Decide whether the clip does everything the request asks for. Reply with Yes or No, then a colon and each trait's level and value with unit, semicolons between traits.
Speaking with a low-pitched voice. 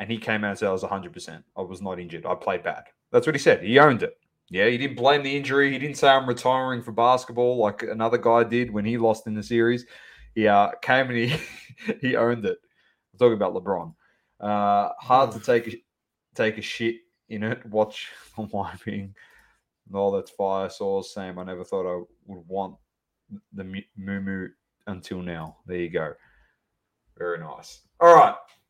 Yes: low, 110 Hz